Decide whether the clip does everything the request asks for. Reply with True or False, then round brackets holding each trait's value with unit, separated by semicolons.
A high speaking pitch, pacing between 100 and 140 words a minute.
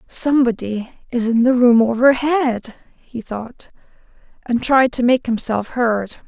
True (240 Hz; 135 wpm)